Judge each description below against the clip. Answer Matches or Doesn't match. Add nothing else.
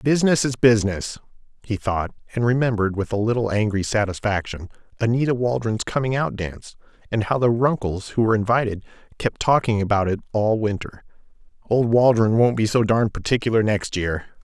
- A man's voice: Matches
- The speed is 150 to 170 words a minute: Matches